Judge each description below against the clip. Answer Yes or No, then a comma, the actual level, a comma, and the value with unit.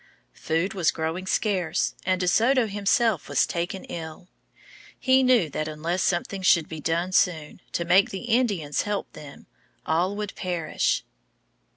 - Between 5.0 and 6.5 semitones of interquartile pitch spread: No, average, 3.9 semitones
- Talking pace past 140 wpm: Yes, average, 150 wpm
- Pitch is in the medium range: Yes, medium, 180 Hz